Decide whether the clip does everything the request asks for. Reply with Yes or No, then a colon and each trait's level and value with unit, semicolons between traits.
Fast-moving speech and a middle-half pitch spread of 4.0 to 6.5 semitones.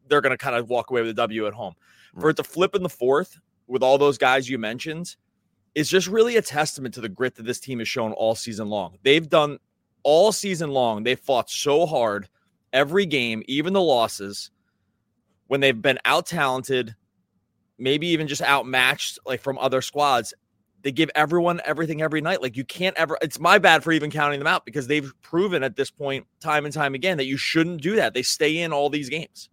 Yes: fast, 215 wpm; average, 4.5 semitones